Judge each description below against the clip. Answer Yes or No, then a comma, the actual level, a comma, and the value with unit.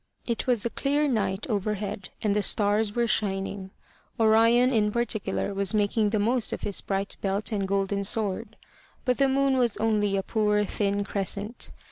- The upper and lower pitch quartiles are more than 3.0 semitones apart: No, narrow, 2.5 semitones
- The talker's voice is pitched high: Yes, high, 210 Hz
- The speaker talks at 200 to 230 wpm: No, average, 170 wpm